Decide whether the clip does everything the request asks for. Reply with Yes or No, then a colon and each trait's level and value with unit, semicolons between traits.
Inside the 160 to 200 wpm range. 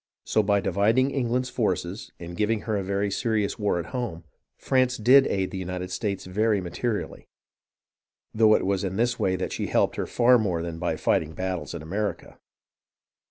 Yes: average, 180 wpm